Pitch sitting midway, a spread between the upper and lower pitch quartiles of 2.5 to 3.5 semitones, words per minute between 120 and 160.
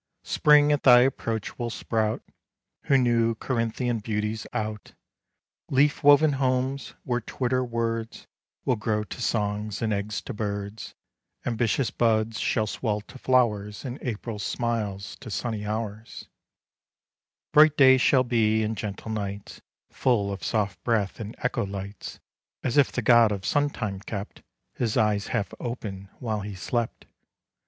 No: low, 115 Hz; average, 2.9 semitones; average, 145 wpm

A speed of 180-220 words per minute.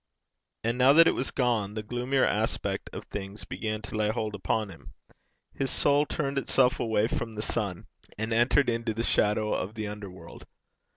Yes: average, 185 wpm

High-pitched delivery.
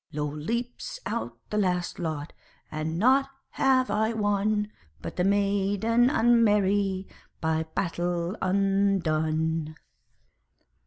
Yes: high, 195 Hz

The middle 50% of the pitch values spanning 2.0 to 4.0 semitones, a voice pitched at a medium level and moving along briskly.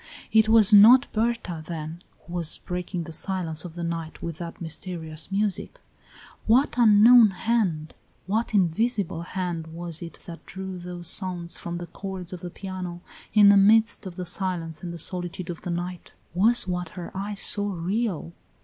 No: average, 3.2 semitones; medium, 180 Hz; average, 170 wpm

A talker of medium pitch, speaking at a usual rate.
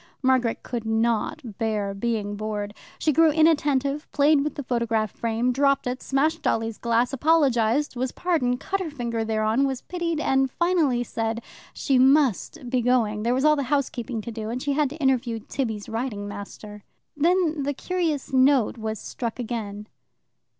No: very high, 250 Hz; average, 165 wpm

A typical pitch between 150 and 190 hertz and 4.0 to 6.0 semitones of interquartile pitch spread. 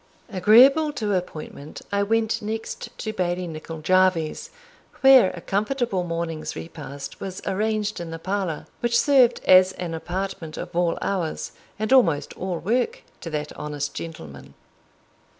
Yes: medium, 185 Hz; average, 4.8 semitones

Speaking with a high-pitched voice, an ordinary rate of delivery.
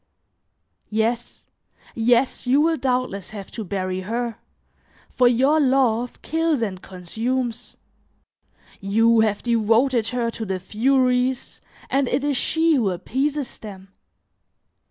No: high, 235 Hz; slow, 115 wpm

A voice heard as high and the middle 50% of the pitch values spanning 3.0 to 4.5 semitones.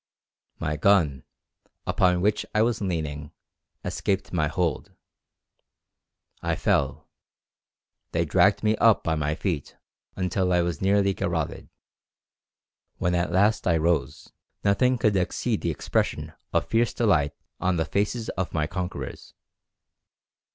No: very low, 90 Hz; average, 3.9 semitones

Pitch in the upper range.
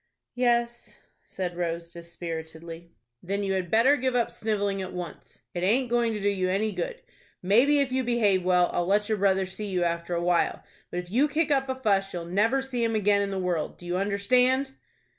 Yes: high, 200 Hz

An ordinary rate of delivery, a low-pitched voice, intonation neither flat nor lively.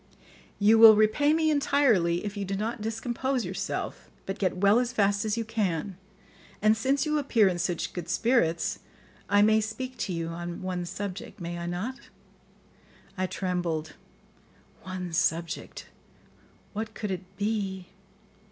No: average, 150 wpm; high, 205 Hz; average, 3.9 semitones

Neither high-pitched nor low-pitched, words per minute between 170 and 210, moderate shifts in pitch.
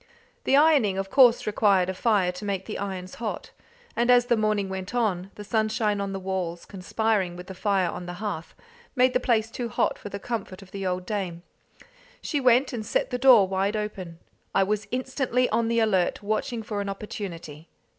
No: high, 205 Hz; average, 200 wpm; average, 3.6 semitones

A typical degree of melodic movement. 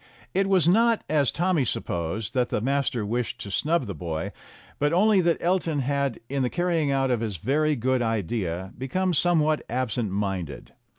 No: wide, 7.1 semitones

